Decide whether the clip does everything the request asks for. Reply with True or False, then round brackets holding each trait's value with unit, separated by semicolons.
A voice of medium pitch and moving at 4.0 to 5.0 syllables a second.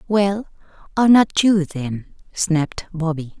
True (180 Hz; 4.3 syllables/s)